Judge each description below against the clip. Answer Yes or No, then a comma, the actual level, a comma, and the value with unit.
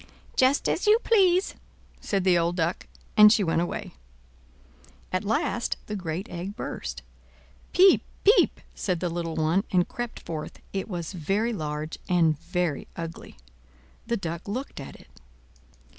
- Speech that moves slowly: No, average, 145 wpm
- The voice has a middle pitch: Yes, medium, 180 Hz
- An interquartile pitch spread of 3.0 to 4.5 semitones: No, average, 4.9 semitones